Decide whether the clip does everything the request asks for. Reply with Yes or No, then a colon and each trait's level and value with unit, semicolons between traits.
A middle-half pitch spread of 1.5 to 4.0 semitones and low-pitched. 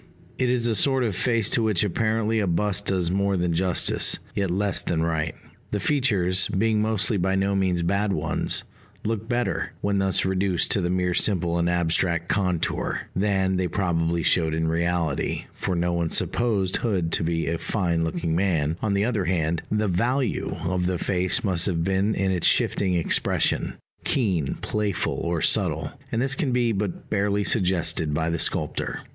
Yes: average, 3.4 semitones; very low, 95 Hz